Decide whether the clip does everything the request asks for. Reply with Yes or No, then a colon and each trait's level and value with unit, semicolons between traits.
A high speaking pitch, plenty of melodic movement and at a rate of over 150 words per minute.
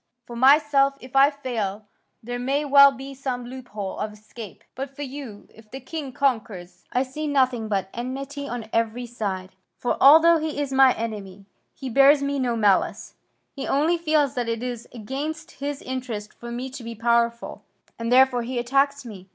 No: very high, 255 Hz; average, 3.3 semitones; average, 180 wpm